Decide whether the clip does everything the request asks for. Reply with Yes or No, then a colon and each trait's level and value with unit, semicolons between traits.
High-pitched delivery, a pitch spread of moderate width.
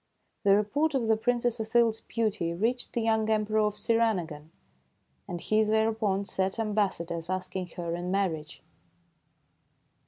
Yes: high, 215 Hz; average, 3.3 semitones